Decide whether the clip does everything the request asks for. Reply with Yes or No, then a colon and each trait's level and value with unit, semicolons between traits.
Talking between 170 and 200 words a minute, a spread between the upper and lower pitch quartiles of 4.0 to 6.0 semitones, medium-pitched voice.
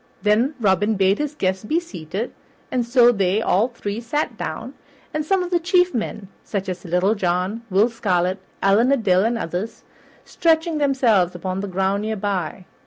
No: average, 175 wpm; average, 4.7 semitones; high, 210 Hz